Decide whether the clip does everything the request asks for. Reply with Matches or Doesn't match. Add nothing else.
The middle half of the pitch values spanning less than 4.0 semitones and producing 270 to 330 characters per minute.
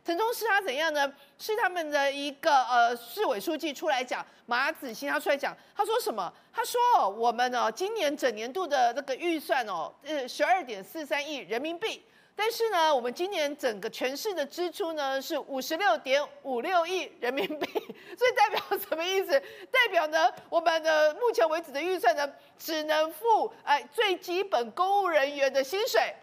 Doesn't match